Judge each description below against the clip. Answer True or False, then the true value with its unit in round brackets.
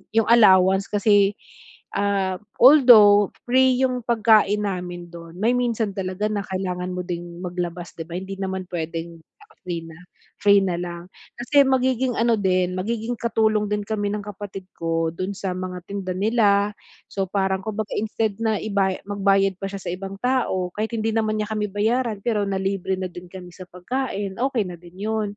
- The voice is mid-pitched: False (200 Hz)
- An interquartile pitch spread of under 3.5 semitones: True (3.0 semitones)